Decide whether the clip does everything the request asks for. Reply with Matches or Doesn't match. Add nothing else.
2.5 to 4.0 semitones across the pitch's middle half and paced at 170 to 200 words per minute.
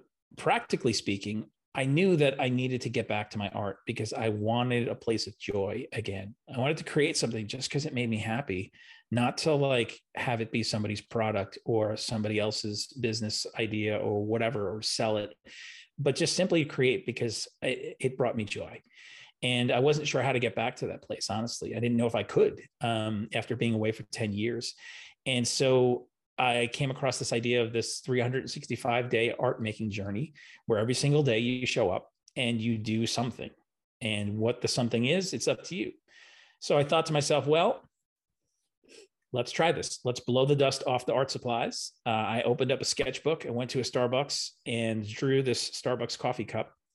Matches